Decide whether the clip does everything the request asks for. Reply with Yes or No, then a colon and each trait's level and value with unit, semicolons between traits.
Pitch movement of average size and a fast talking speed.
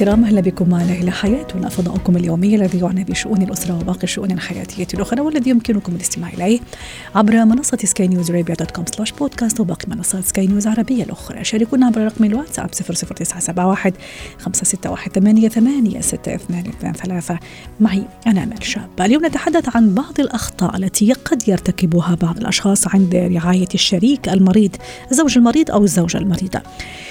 Yes: average, 3.7 semitones; fast, 140 wpm